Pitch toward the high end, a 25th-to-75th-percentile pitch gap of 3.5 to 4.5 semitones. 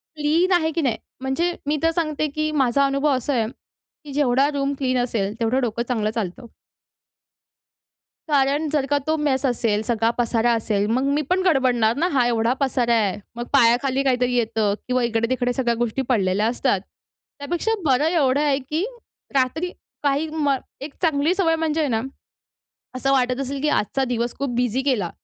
Yes: very high, 265 Hz; average, 3.8 semitones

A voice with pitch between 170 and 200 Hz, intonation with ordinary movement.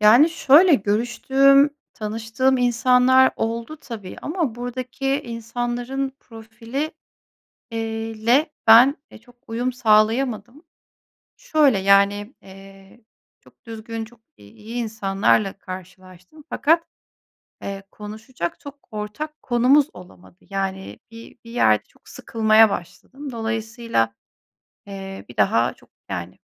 No: high, 230 Hz; average, 4.0 semitones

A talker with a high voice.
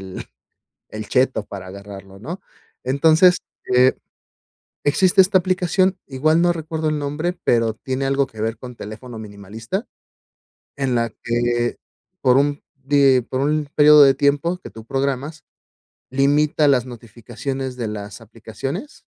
No: low, 135 Hz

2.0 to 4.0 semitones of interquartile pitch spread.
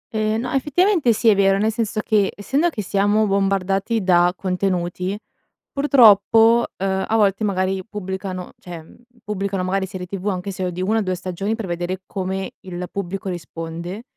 Yes: average, 2.7 semitones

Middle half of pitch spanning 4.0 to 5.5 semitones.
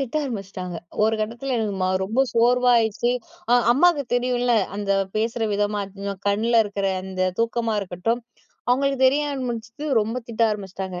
No: average, 3.4 semitones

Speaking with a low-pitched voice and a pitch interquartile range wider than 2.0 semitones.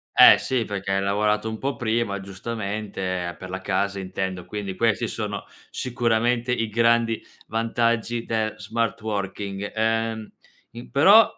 Yes: low, 110 Hz; average, 2.8 semitones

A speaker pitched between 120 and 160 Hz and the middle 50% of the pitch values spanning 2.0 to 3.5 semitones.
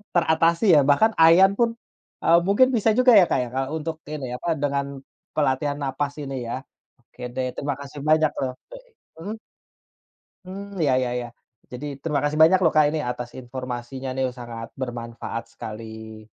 No: medium, 140 Hz; average, 4.7 semitones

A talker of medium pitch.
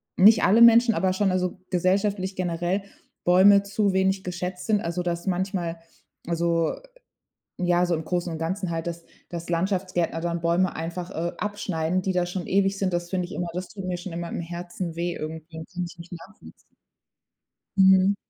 Yes: medium, 180 Hz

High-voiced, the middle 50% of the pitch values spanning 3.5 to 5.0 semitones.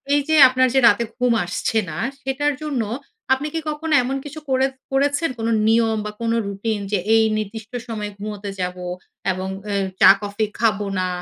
Yes: high, 225 Hz; average, 4.6 semitones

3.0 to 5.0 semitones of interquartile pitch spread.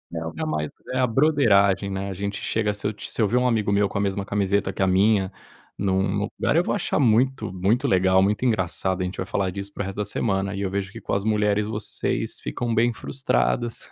No: narrow, 2.4 semitones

